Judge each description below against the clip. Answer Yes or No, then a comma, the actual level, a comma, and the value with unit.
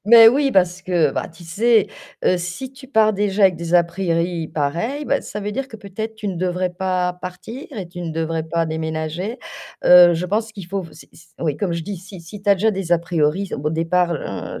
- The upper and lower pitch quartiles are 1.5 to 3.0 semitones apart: No, average, 3.8 semitones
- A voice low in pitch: No, medium, 180 Hz